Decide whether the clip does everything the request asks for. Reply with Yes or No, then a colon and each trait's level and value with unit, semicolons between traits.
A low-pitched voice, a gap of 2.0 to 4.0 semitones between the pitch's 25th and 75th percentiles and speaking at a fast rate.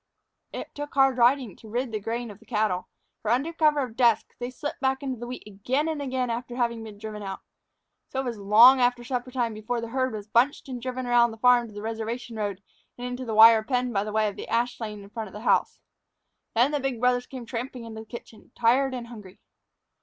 No: high, 240 Hz; narrow, 2.6 semitones; fast, 240 wpm